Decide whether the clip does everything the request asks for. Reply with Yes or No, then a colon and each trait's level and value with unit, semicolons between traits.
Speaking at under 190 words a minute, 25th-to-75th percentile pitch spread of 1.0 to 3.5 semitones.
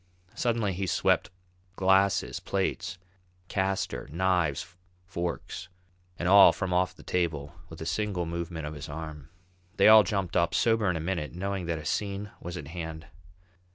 Yes: average, 155 wpm; average, 3.1 semitones